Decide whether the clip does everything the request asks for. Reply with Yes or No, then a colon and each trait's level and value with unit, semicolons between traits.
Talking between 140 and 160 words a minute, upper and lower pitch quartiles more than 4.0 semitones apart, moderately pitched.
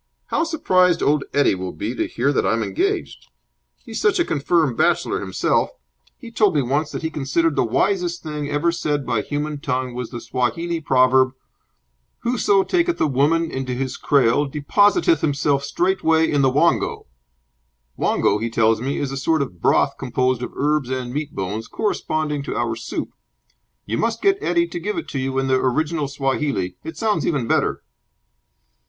No: average, 175 wpm; average, 4.6 semitones; medium, 145 Hz